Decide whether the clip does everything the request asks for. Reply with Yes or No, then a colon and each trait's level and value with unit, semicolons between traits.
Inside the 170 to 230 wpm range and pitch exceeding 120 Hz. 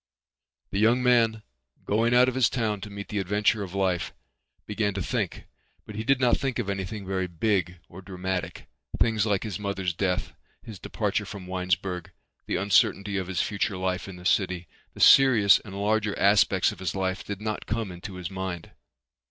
No: average, 185 wpm; low, 100 Hz